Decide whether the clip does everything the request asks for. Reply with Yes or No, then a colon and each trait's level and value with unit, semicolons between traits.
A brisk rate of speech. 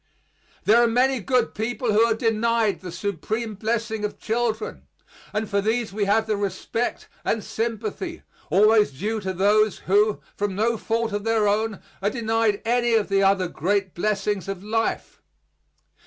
No: average, 160 wpm